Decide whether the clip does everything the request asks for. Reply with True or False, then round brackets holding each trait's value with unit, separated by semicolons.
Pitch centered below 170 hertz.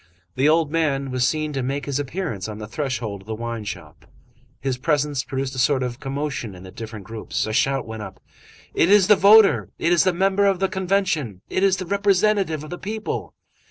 True (140 Hz)